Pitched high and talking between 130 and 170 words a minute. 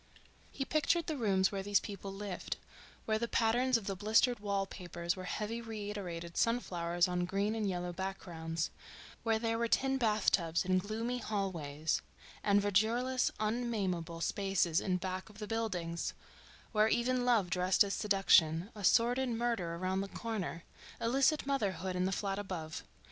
Yes: high, 200 Hz; average, 150 wpm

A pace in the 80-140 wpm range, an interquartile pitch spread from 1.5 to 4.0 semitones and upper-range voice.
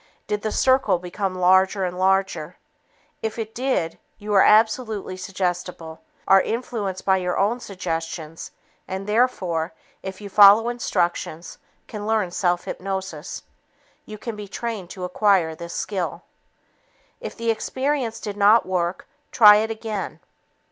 Yes: slow, 135 wpm; average, 3.4 semitones; high, 195 Hz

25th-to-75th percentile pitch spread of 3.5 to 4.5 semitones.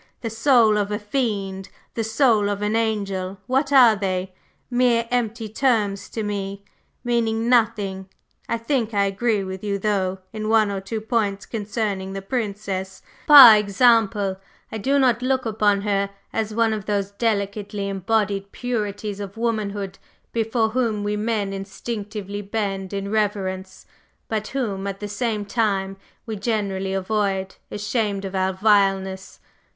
No: narrow, 2.4 semitones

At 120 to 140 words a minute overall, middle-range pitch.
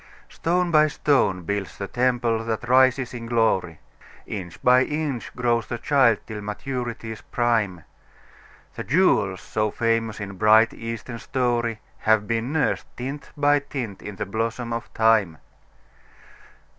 No: slow, 135 wpm; low, 115 Hz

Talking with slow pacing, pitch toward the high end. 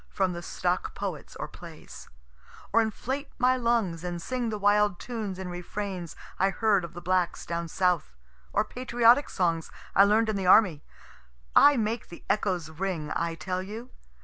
No: average, 170 wpm; high, 195 Hz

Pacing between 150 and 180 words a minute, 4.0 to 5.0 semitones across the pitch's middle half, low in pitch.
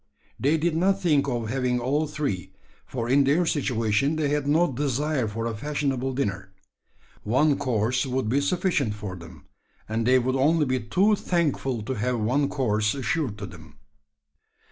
Yes: average, 165 wpm; average, 4.7 semitones; low, 130 Hz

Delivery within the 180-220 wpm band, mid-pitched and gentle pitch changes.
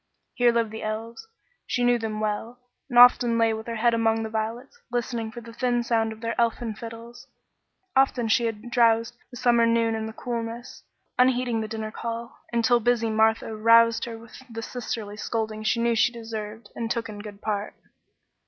No: average, 190 wpm; high, 230 Hz; narrow, 1.4 semitones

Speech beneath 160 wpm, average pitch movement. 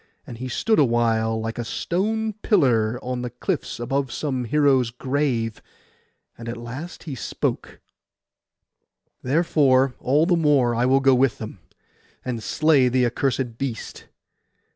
Yes: average, 140 wpm; average, 3.5 semitones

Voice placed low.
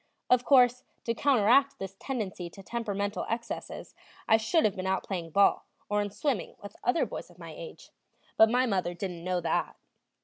No: high, 210 Hz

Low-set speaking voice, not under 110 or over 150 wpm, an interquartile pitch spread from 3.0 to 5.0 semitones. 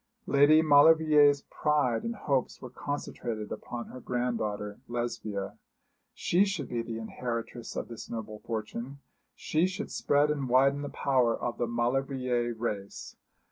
Yes: low, 125 Hz; average, 140 wpm; average, 3.6 semitones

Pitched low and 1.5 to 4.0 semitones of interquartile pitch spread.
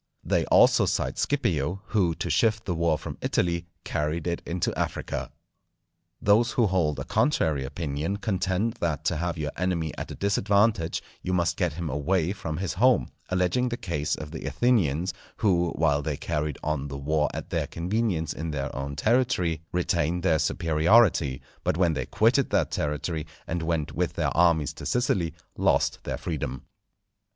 Yes: very low, 85 Hz; average, 3.6 semitones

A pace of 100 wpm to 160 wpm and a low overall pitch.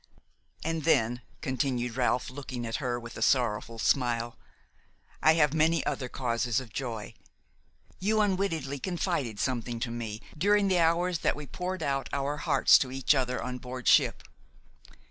Yes: average, 155 wpm; low, 130 Hz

